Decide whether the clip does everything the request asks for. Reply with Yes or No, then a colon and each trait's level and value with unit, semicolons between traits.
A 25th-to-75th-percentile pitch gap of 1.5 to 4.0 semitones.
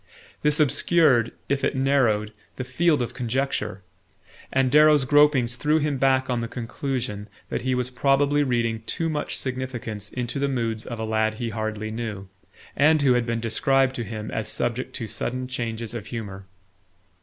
Yes: average, 3.4 semitones